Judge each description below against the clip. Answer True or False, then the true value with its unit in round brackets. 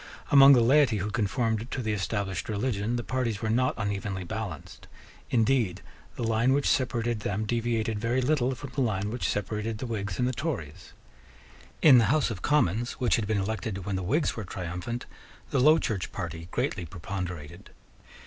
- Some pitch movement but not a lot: True (3.9 semitones)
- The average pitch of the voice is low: True (110 Hz)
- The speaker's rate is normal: True (175 wpm)